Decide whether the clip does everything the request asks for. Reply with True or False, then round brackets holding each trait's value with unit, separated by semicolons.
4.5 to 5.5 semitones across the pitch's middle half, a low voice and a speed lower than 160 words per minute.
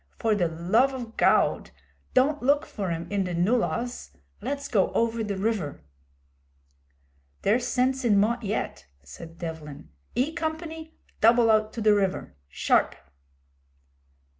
False (5.0 semitones; 220 Hz; 135 wpm)